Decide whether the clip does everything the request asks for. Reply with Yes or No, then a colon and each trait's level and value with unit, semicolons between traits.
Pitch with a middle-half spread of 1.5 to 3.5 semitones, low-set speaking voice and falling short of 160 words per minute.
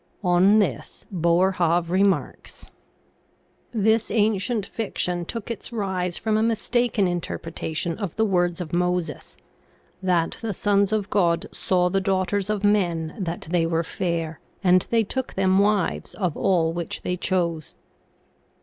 No: average, 3.1 semitones; medium, 185 Hz; average, 150 wpm